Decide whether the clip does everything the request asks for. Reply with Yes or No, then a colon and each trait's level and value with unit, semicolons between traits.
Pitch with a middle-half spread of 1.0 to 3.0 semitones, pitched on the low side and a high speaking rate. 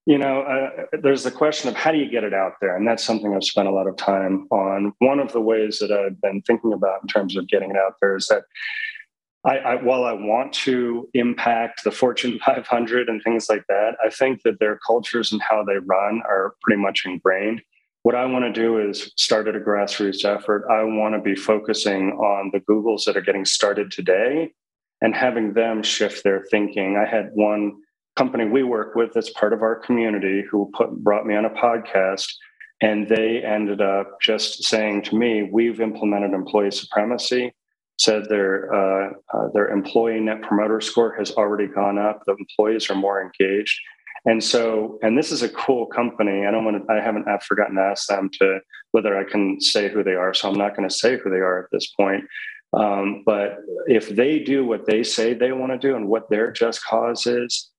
Yes: average, 2.7 semitones; low, 110 Hz; fast, 215 wpm